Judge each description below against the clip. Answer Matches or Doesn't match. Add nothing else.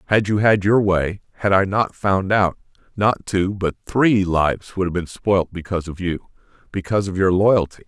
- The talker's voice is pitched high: Doesn't match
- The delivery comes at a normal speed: Matches